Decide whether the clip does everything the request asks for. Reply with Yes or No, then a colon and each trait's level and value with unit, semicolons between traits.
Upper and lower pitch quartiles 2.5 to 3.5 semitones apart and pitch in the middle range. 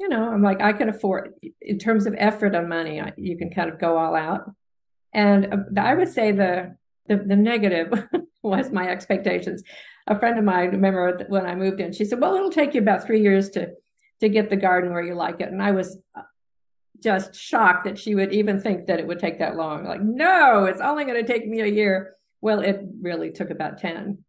No: average, 2.8 semitones; high, 200 Hz